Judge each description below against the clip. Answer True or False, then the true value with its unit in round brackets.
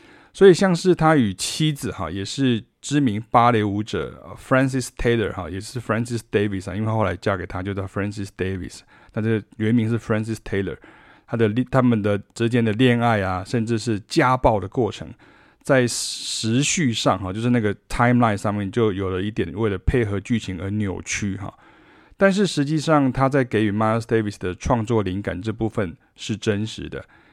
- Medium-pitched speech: False (110 Hz)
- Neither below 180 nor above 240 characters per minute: False (370 characters per minute)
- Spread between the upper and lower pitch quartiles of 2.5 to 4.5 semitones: True (3.8 semitones)